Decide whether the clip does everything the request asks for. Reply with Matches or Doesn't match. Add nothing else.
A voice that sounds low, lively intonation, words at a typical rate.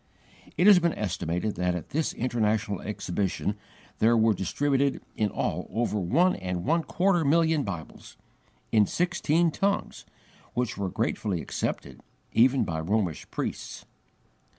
Doesn't match